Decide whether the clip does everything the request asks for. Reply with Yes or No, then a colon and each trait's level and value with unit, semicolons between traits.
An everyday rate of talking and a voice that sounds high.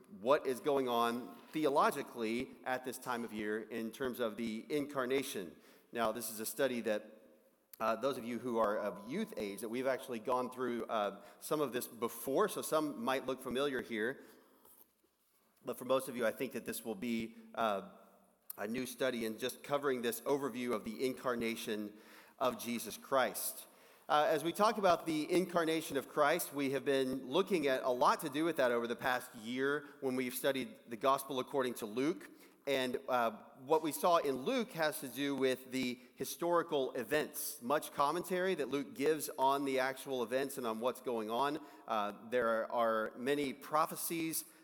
No: average, 185 wpm; low, 130 Hz